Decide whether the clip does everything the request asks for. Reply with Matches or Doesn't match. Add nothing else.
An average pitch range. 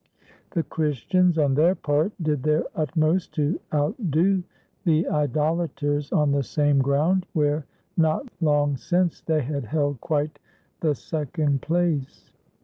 Doesn't match